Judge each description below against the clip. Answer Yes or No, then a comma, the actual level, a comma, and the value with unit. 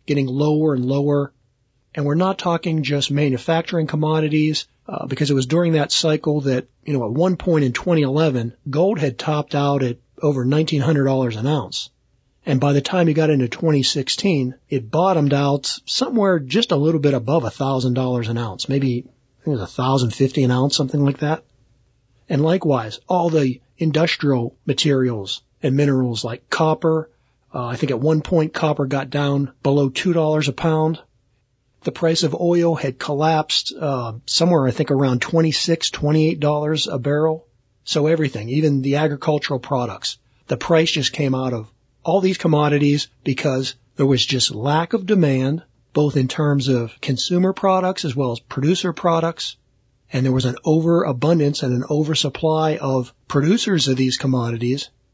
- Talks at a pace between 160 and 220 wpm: Yes, average, 165 wpm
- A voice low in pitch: No, medium, 145 Hz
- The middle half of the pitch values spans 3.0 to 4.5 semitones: Yes, average, 3.4 semitones